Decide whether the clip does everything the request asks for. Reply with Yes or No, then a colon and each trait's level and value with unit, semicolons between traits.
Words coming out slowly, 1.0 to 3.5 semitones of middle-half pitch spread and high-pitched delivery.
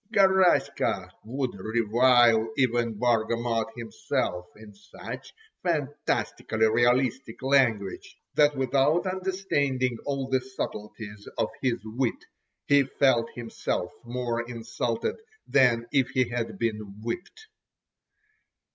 No: slow, 100 wpm; average, 3.1 semitones; low, 120 Hz